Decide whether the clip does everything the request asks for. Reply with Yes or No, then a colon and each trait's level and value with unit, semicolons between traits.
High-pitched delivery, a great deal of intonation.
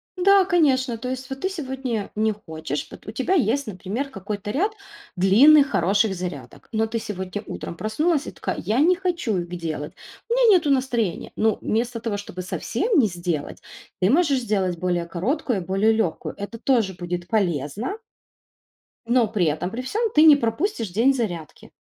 Yes: high, 220 Hz; wide, 6.8 semitones